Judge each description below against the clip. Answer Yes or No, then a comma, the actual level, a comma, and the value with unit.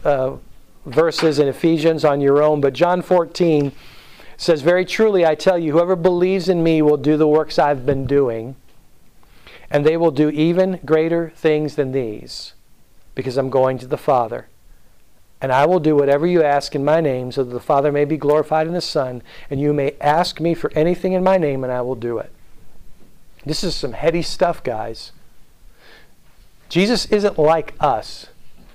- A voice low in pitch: No, medium, 150 Hz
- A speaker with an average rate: Yes, average, 180 wpm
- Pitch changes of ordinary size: Yes, average, 3.3 semitones